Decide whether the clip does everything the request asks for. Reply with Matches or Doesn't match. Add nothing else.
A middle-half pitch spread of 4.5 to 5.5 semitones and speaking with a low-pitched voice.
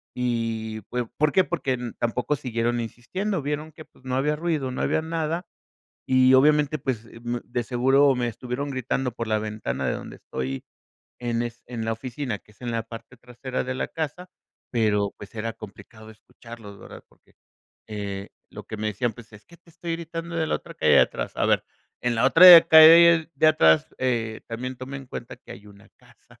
Matches